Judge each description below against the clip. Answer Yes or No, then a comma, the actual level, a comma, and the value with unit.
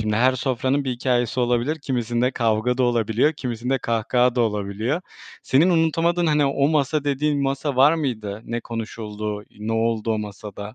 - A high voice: No, low, 125 Hz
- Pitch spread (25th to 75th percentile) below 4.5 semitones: Yes, average, 3.9 semitones